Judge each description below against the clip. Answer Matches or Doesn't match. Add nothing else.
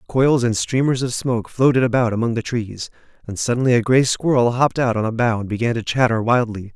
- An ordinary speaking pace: Doesn't match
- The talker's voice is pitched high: Doesn't match